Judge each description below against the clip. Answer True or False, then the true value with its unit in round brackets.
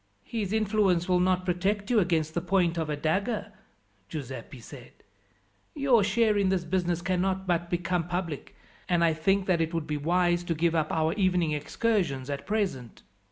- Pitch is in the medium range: True (175 Hz)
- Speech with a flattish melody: False (3.0 semitones)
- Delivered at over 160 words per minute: True (175 wpm)